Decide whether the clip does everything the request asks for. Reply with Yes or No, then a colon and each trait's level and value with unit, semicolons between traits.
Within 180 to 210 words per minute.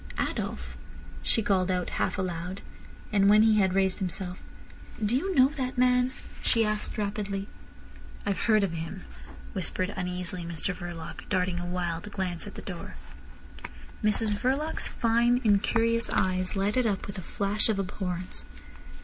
No: average, 150 wpm